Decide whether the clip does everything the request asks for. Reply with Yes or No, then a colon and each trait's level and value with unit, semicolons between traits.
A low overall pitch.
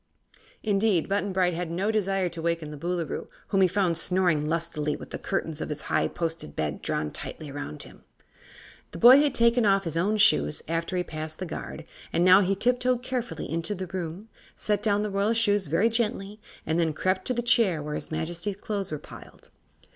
No: medium, 185 Hz